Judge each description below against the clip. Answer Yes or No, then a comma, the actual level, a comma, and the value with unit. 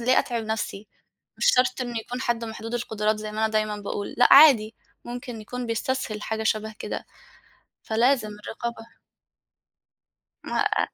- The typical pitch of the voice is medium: No, high, 225 Hz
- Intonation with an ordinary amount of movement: No, narrow, 2.1 semitones